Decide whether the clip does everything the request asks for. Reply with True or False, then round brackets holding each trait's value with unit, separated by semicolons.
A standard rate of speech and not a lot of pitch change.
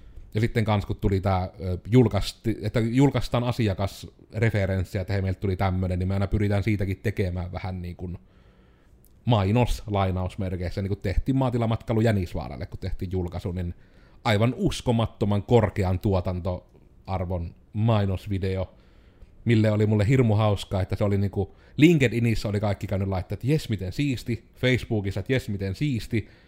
False (140 wpm; 3.3 semitones)